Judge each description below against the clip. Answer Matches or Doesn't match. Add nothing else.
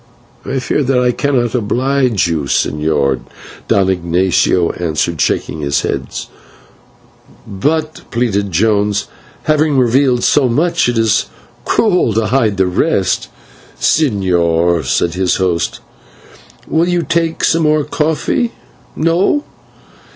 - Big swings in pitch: Matches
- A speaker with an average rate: Doesn't match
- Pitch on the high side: Doesn't match